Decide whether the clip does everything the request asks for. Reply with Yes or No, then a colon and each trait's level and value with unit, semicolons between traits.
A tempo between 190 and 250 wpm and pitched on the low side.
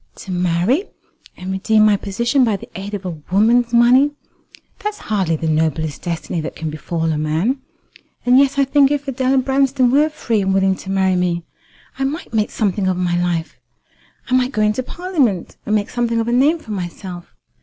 No: average, 195 wpm; high, 210 Hz